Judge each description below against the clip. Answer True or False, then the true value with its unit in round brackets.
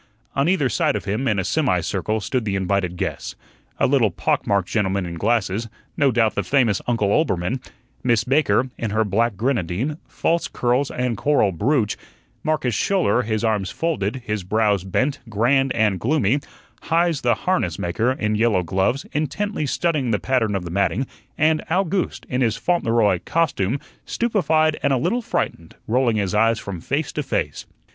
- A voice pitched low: True (115 Hz)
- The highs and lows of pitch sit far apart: True (5.7 semitones)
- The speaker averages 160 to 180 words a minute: True (170 wpm)